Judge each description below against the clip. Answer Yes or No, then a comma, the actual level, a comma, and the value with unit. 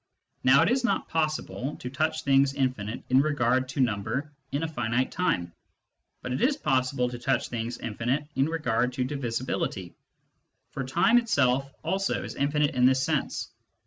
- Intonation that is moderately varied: Yes, average, 3.3 semitones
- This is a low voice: Yes, low, 130 Hz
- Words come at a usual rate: Yes, average, 165 wpm